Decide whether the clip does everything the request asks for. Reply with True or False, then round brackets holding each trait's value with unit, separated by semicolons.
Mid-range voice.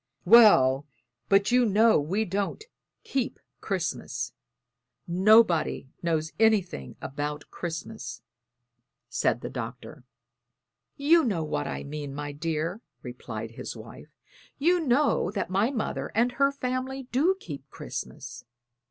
True (180 Hz)